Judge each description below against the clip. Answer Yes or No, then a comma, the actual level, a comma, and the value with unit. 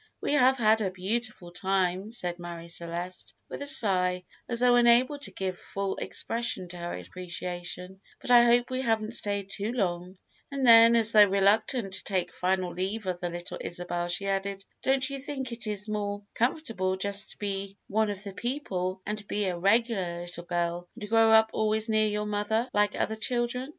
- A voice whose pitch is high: Yes, high, 205 Hz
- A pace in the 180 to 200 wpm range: Yes, average, 190 wpm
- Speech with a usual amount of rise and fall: Yes, average, 4.0 semitones